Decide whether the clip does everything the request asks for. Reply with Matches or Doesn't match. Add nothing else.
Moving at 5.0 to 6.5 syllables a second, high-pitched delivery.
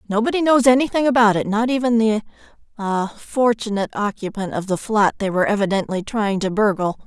Matches